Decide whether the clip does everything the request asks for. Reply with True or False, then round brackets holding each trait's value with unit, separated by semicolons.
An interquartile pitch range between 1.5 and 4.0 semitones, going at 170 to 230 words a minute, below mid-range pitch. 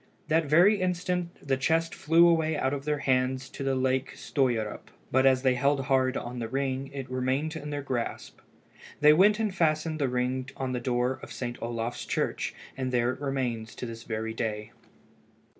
True (3.4 semitones; 190 wpm; 130 Hz)